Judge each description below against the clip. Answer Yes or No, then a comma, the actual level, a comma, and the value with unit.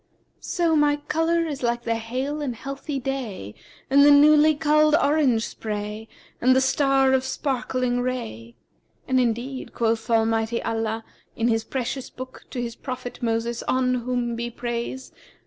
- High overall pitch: Yes, very high, 255 Hz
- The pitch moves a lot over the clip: No, average, 3.2 semitones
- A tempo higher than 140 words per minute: Yes, average, 150 wpm